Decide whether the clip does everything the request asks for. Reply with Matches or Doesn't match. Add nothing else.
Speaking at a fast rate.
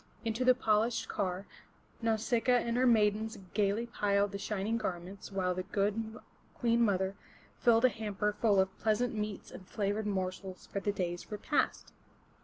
Doesn't match